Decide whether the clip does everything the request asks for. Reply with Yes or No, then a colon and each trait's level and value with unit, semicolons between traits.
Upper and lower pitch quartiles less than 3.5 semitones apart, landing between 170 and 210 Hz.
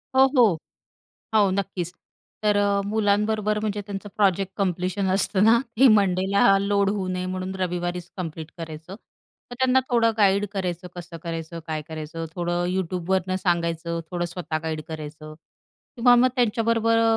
Yes: average, 3.1 semitones; high, 190 Hz